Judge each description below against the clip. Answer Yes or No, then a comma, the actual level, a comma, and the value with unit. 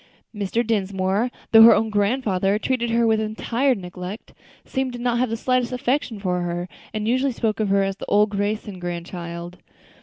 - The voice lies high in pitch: Yes, high, 215 Hz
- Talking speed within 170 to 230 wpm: Yes, average, 175 wpm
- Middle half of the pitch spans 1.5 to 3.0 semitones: No, average, 3.6 semitones